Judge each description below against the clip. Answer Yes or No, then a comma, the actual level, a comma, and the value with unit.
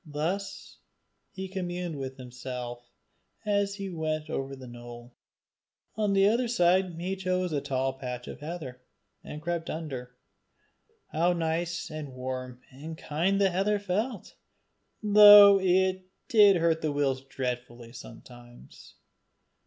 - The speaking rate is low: Yes, slow, 130 wpm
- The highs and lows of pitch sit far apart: Yes, wide, 6.4 semitones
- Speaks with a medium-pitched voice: Yes, medium, 160 Hz